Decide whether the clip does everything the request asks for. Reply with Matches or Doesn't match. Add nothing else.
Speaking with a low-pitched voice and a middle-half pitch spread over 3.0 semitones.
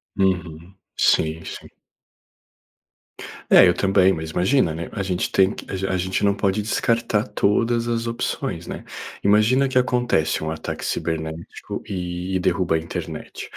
Matches